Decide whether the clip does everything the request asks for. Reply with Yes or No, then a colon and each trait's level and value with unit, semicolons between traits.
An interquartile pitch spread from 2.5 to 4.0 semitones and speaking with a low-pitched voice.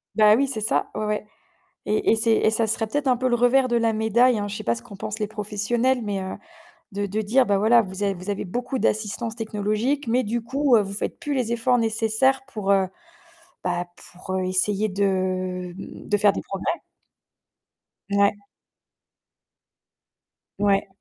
No: average, 3.1 semitones; high, 215 Hz